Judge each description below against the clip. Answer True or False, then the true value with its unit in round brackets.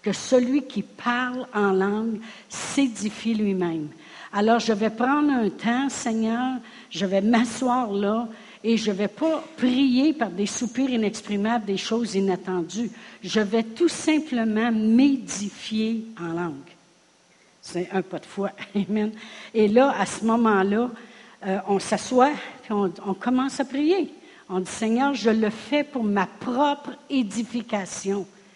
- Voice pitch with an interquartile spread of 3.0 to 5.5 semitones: True (3.9 semitones)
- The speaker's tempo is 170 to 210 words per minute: False (145 wpm)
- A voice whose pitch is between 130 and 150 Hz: False (225 Hz)